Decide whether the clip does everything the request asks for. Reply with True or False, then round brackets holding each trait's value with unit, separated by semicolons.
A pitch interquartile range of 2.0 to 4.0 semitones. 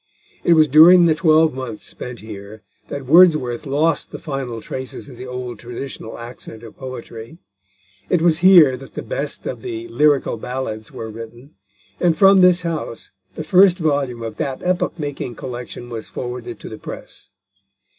False (5.3 semitones)